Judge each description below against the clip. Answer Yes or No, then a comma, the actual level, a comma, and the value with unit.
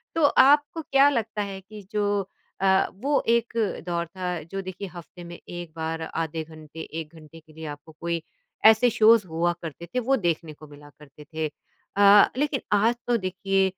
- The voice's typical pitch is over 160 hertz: Yes, medium, 185 Hz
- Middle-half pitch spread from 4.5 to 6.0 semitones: Yes, average, 5.0 semitones